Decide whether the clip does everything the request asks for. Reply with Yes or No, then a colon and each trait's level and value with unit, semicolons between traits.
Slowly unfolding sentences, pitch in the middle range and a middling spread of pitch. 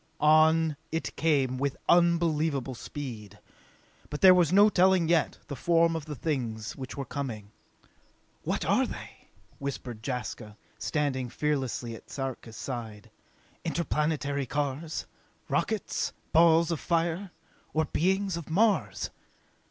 Yes: slow, 120 wpm; medium, 150 Hz; average, 4.2 semitones